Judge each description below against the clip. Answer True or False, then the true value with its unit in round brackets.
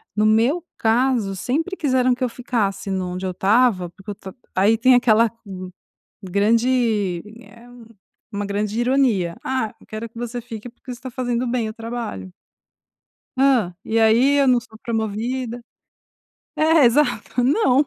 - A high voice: True (230 Hz)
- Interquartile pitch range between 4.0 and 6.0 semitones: False (3.3 semitones)